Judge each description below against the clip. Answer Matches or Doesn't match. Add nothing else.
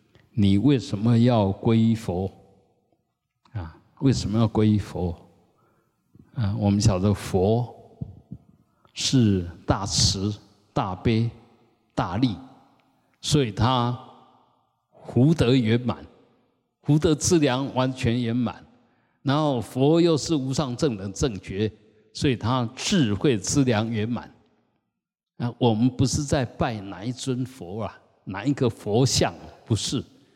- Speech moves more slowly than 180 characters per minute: Matches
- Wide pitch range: Doesn't match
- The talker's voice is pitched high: Doesn't match